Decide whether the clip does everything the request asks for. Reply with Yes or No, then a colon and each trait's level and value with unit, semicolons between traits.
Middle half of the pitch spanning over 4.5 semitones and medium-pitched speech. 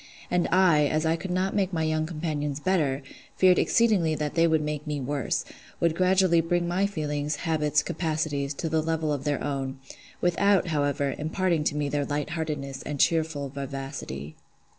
No: average, 2.9 semitones; medium, 155 Hz